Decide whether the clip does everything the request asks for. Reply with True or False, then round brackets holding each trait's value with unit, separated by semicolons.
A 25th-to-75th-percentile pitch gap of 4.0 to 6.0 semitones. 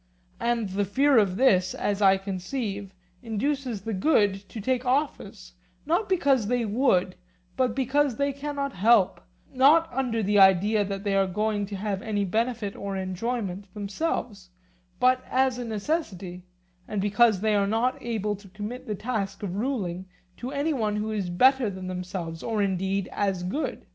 True (4.5 semitones)